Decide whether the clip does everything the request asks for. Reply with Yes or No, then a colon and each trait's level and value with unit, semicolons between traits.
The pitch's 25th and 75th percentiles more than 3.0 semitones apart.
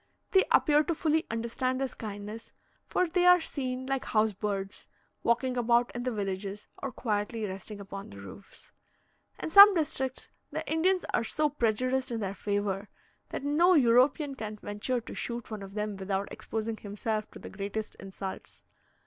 Yes: average, 4.6 semitones